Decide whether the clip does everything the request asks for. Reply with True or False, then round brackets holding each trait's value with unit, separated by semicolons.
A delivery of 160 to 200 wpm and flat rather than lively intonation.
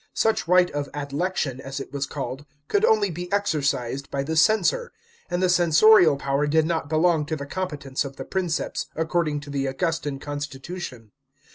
False (180 wpm; 4.2 semitones)